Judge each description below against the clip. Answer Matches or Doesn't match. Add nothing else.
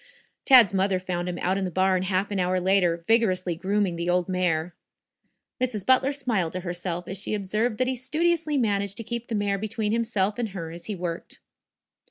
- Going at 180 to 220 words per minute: Matches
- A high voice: Matches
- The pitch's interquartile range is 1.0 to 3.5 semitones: Doesn't match